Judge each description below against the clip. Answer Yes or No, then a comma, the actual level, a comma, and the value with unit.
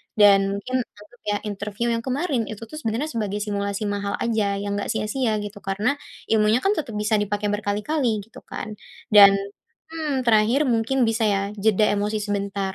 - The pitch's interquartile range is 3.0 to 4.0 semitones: No, narrow, 2.4 semitones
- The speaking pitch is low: No, high, 215 Hz